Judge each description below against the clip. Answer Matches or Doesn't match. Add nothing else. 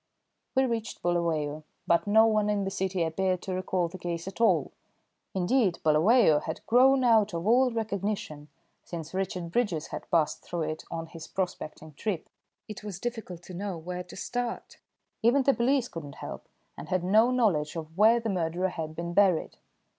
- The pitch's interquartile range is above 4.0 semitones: Matches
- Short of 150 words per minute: Doesn't match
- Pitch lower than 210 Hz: Matches